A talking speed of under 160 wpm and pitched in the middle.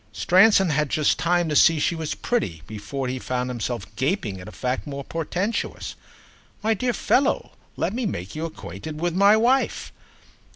No: average, 170 wpm; medium, 155 Hz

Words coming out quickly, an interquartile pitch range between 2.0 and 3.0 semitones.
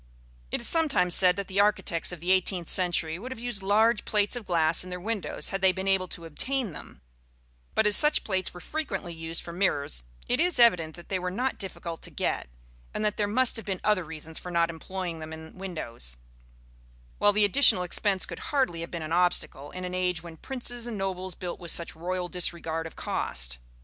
No: fast, 215 wpm; average, 3.6 semitones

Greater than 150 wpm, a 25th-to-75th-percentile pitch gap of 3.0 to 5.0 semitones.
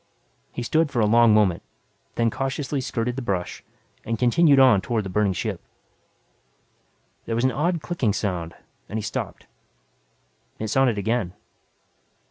No: average, 145 wpm; average, 4.2 semitones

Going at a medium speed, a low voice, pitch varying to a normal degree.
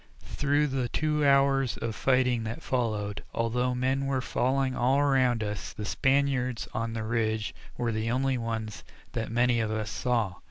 Yes: average, 165 wpm; low, 125 Hz; average, 3.2 semitones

